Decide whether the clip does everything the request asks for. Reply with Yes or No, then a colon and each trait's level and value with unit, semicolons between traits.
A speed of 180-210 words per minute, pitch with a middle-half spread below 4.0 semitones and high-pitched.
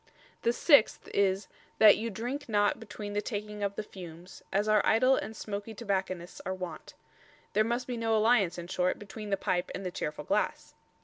Yes: average, 190 wpm; average, 2.9 semitones; high, 205 Hz